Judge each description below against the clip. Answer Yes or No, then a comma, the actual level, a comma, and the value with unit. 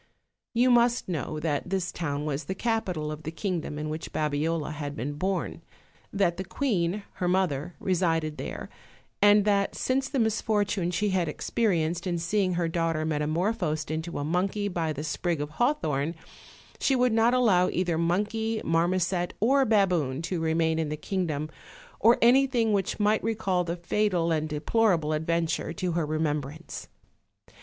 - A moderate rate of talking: Yes, average, 160 wpm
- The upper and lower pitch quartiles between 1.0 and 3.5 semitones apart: No, average, 4.7 semitones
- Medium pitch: Yes, medium, 175 Hz